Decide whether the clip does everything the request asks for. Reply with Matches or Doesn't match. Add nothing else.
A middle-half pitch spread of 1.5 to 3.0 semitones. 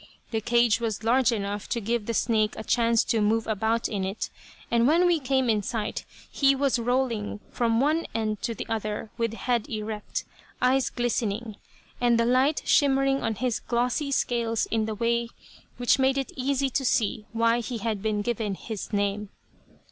Matches